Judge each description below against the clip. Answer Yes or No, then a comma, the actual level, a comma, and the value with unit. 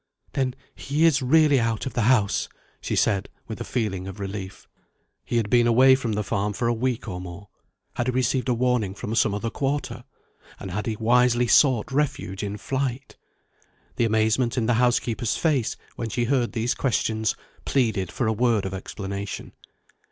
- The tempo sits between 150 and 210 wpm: Yes, average, 180 wpm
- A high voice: No, low, 115 Hz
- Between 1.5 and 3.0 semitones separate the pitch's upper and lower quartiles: No, average, 3.4 semitones